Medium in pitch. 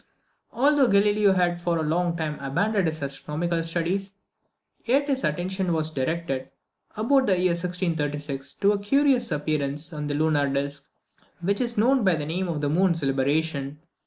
Yes: medium, 170 Hz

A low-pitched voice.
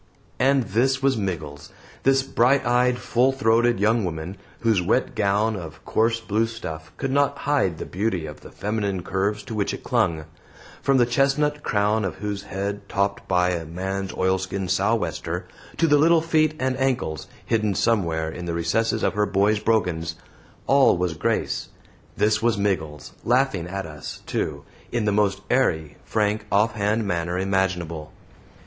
Yes: low, 105 Hz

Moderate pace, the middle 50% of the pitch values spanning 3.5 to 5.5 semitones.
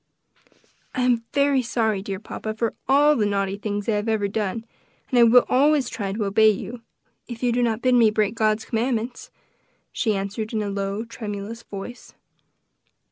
No: average, 180 wpm; average, 2.8 semitones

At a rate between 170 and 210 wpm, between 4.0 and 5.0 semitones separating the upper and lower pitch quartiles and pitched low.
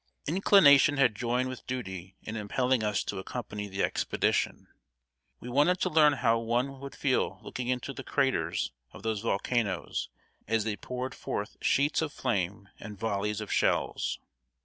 No: average, 155 wpm; average, 4.3 semitones; low, 120 Hz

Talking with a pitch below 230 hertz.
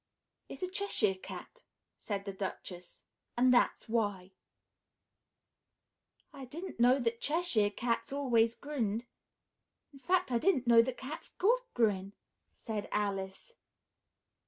No: high, 235 Hz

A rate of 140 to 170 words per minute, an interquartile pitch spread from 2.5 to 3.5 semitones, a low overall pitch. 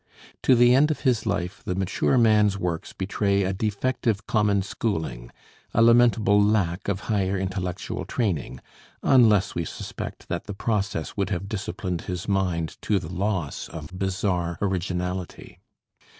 Yes: average, 145 wpm; average, 3.0 semitones; low, 100 Hz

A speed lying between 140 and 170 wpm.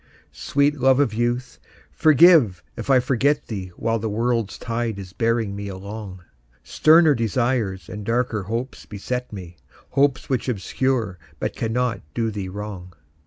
Yes: average, 145 wpm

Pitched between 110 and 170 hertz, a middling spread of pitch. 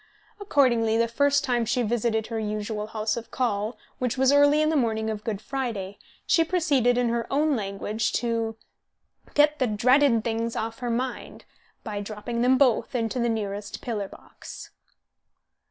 No: high, 230 Hz; average, 3.0 semitones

